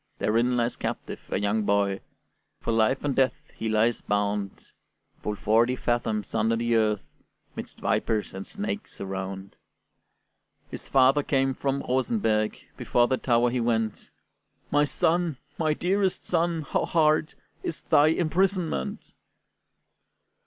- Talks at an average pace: No, slow, 130 wpm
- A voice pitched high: No, low, 125 Hz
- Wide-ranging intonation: Yes, wide, 6.2 semitones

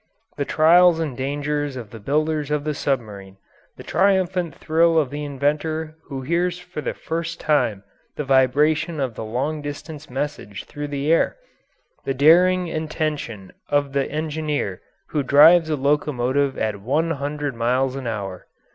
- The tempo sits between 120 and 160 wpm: Yes, average, 155 wpm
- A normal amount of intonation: Yes, average, 3.1 semitones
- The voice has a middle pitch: Yes, medium, 145 Hz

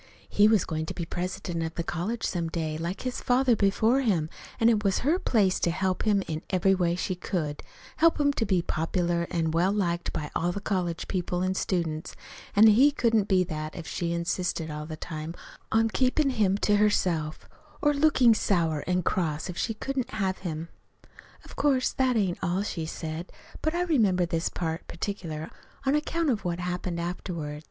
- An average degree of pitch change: Yes, average, 4.6 semitones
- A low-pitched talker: No, medium, 185 Hz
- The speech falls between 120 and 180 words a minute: No, average, 195 wpm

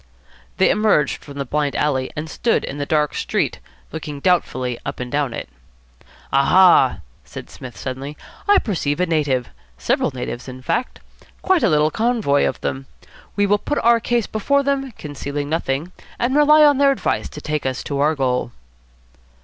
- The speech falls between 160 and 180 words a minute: Yes, average, 175 wpm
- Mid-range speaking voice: Yes, medium, 150 Hz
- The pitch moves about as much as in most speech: No, wide, 8.0 semitones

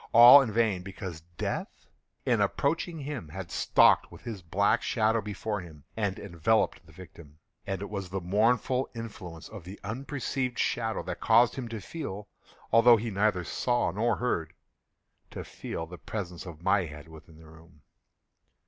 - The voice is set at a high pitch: No, low, 100 Hz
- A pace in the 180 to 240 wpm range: No, average, 155 wpm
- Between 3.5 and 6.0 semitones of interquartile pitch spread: Yes, average, 5.0 semitones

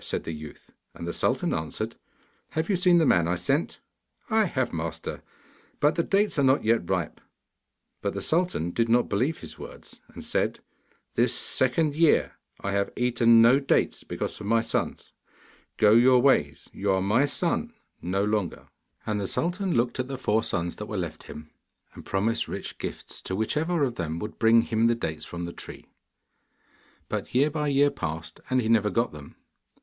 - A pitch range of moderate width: No, wide, 7.0 semitones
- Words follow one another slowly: No, average, 185 wpm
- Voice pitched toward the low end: Yes, low, 115 Hz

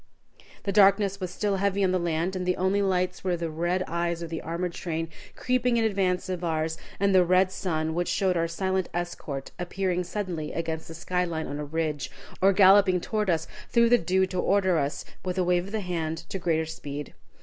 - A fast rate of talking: Yes, fast, 215 wpm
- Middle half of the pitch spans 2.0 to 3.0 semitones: Yes, narrow, 2.6 semitones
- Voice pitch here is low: No, medium, 180 Hz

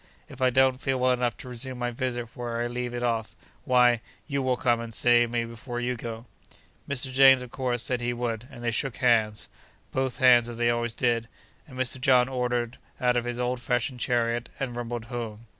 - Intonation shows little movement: Yes, narrow, 1.3 semitones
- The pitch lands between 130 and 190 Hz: No, low, 120 Hz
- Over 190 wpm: Yes, average, 200 wpm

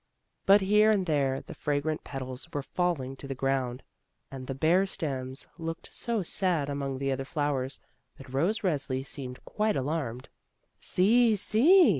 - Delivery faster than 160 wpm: No, average, 155 wpm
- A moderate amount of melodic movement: No, wide, 5.9 semitones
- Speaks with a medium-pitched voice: Yes, medium, 145 Hz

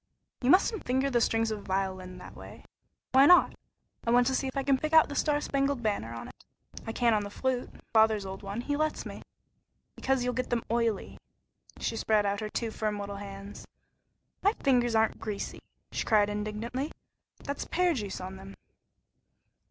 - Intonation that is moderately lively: Yes, average, 4.6 semitones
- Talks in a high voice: Yes, high, 225 Hz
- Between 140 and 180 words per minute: No, average, 190 wpm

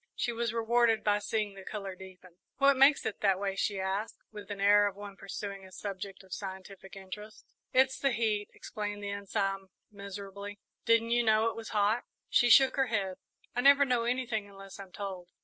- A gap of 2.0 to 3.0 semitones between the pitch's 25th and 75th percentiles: Yes, average, 2.7 semitones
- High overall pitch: Yes, high, 205 Hz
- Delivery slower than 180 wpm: No, average, 195 wpm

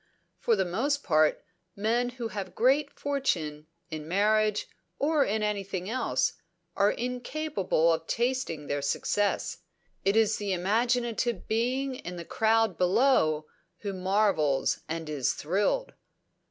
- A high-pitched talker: Yes, high, 210 Hz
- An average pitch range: No, wide, 5.9 semitones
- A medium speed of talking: No, slow, 130 wpm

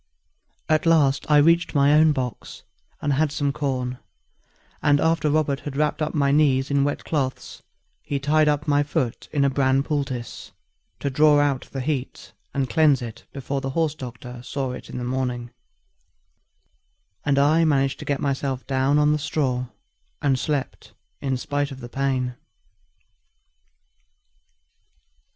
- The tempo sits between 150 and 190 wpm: Yes, average, 155 wpm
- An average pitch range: No, narrow, 2.1 semitones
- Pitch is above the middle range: No, medium, 140 Hz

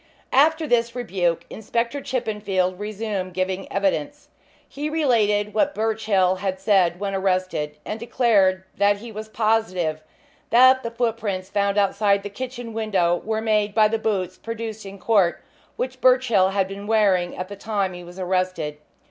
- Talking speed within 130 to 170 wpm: Yes, average, 155 wpm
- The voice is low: No, high, 205 Hz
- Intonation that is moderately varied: Yes, average, 3.3 semitones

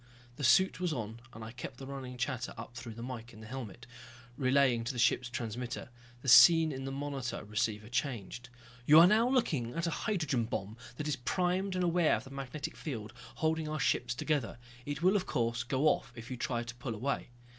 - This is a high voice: No, low, 130 Hz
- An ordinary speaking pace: No, fast, 210 wpm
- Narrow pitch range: No, average, 4.5 semitones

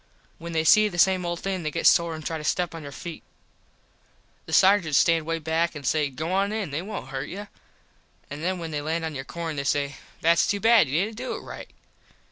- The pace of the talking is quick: Yes, fast, 240 wpm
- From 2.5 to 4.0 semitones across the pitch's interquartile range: Yes, average, 3.5 semitones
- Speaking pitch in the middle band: Yes, medium, 165 Hz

